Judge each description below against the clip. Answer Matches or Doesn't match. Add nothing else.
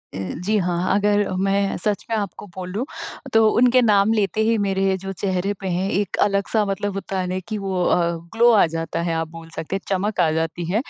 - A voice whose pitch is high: Matches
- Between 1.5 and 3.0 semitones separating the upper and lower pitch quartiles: Matches